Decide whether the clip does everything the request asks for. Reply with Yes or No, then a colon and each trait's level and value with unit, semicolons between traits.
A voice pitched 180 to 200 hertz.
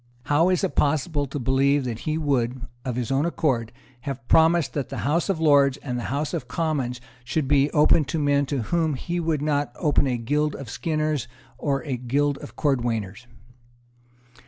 No: medium, 145 Hz